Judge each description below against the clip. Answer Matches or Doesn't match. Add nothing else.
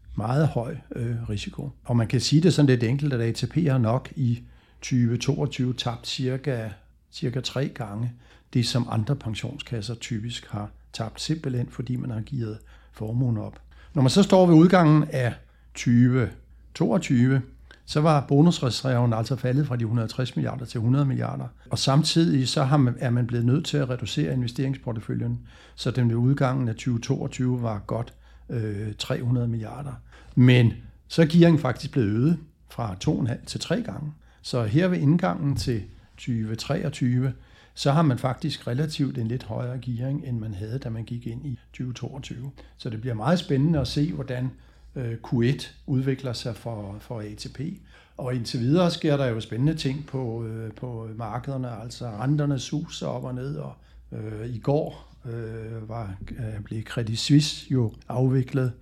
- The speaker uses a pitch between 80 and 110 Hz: Doesn't match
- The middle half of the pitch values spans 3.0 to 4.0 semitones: Matches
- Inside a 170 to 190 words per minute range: Doesn't match